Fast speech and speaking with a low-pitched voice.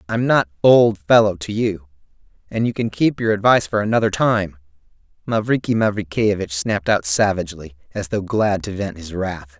No: average, 170 wpm; low, 100 Hz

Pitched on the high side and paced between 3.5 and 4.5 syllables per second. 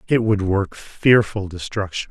No: low, 100 Hz; 4.1 syllables/s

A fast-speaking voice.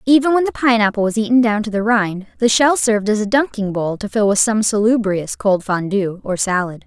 Yes: fast, 225 wpm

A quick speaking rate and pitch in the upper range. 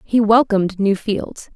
No: average, 155 wpm; high, 210 Hz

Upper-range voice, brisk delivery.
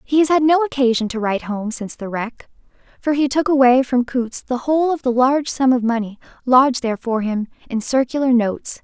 Yes: very high, 255 Hz; fast, 215 wpm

